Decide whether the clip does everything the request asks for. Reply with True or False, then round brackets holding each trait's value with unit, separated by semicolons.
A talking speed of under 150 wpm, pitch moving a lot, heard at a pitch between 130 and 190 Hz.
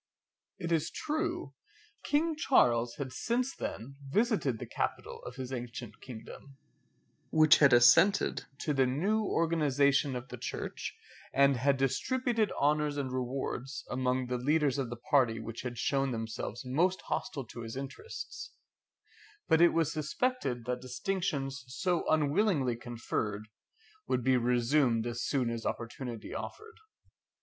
False (135 wpm; 4.5 semitones; 135 Hz)